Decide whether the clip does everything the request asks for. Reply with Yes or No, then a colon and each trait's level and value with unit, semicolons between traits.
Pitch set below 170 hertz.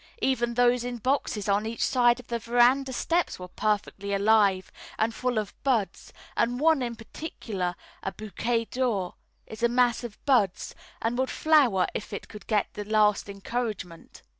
No: high, 230 Hz